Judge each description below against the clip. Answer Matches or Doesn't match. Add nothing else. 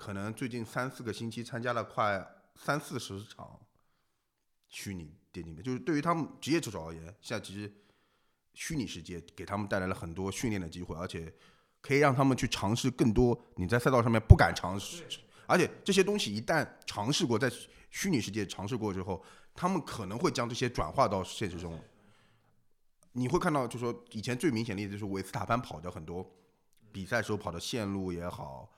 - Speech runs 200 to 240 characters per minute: Doesn't match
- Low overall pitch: Matches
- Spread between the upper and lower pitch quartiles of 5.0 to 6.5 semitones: Doesn't match